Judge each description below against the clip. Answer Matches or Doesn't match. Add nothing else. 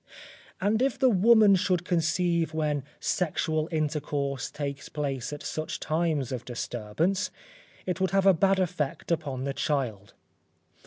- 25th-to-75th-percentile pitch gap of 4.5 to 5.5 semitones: Matches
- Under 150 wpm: Matches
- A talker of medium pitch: Matches